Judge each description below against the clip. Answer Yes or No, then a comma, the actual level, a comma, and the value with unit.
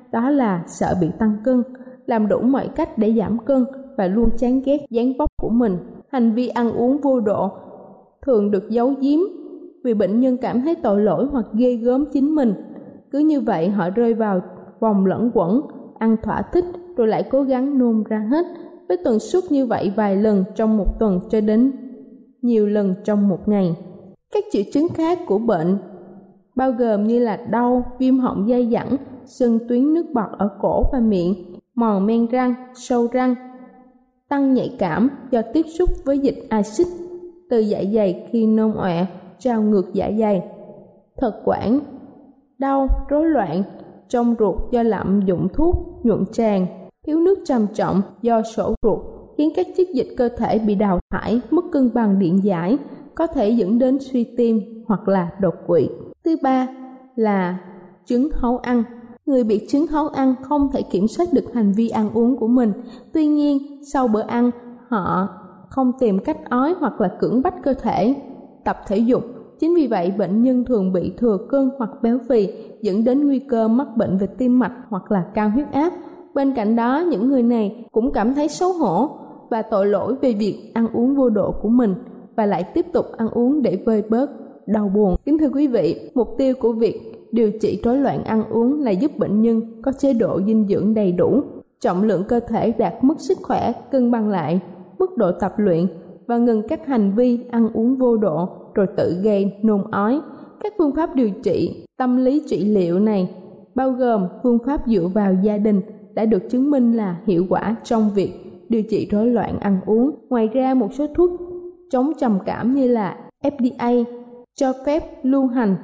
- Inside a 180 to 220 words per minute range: Yes, average, 195 wpm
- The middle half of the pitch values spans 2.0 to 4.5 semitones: Yes, average, 4.2 semitones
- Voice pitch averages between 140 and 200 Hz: No, high, 235 Hz